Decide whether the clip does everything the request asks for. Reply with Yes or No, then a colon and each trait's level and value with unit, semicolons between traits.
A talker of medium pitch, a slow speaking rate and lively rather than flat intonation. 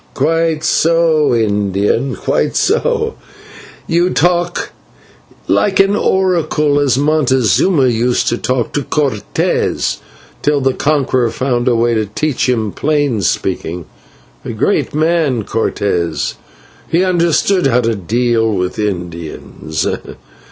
No: low, 130 Hz; slow, 115 wpm; wide, 6.2 semitones